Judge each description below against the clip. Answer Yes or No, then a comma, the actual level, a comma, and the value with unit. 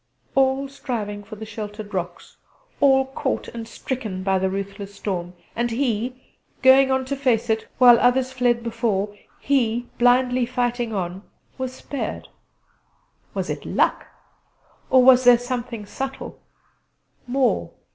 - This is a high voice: Yes, high, 240 Hz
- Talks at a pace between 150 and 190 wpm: No, slow, 135 wpm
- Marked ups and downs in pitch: No, average, 3.6 semitones